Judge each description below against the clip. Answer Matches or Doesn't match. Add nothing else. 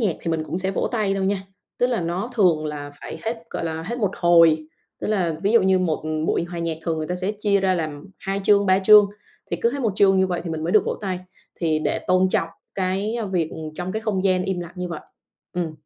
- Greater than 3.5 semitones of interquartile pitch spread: Doesn't match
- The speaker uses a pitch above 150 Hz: Matches